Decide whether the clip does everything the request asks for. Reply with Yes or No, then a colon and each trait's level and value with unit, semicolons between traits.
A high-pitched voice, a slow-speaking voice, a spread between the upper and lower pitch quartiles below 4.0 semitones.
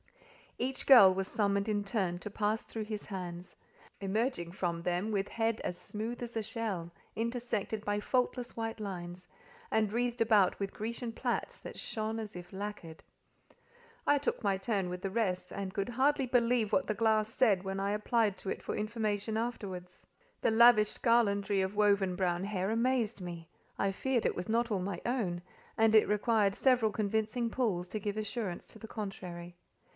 No: high, 210 Hz; average, 175 wpm; average, 3.0 semitones